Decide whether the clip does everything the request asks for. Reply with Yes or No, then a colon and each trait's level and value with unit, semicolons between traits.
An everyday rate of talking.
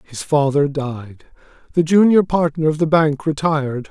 Yes: average, 155 wpm